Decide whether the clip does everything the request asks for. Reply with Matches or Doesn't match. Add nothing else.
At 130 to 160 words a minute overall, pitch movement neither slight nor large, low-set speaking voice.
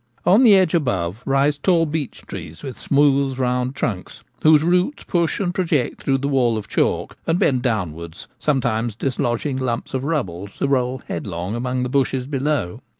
Doesn't match